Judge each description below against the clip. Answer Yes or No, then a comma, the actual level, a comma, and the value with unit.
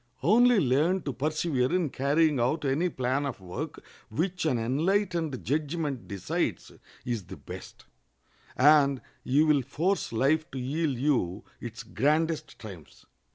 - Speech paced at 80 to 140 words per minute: Yes, slow, 135 wpm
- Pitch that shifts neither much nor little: Yes, average, 4.2 semitones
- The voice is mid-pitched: Yes, medium, 145 Hz